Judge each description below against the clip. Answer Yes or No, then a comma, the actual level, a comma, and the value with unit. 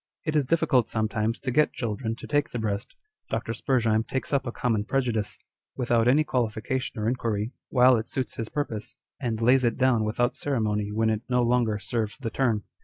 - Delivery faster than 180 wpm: Yes, average, 190 wpm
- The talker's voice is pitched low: Yes, low, 120 Hz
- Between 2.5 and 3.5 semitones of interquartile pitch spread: Yes, average, 2.8 semitones